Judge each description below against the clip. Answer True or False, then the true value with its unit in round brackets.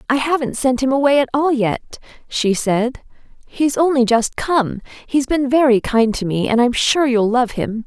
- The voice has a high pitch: True (250 Hz)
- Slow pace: False (200 wpm)